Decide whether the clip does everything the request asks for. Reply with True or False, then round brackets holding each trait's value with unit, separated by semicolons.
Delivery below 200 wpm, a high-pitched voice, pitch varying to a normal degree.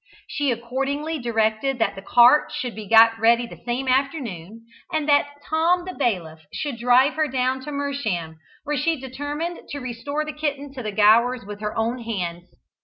True (180 wpm; 250 Hz; 4.4 semitones)